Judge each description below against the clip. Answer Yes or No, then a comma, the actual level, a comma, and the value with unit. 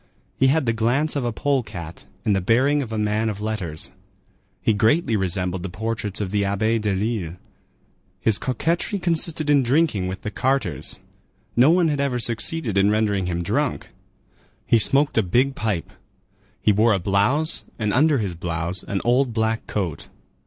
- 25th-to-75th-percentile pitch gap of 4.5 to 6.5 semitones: Yes, wide, 5.5 semitones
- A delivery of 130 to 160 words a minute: No, average, 175 wpm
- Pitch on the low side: Yes, low, 110 Hz